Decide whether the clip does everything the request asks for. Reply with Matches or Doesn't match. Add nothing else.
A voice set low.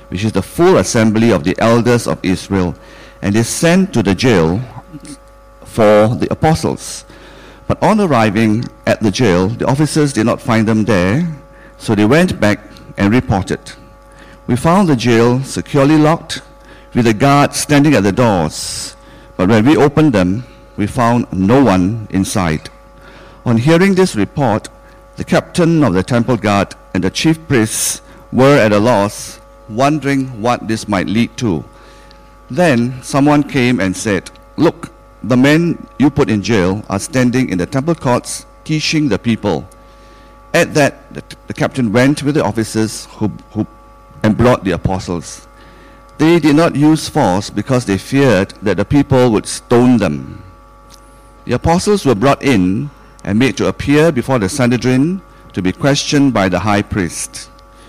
Matches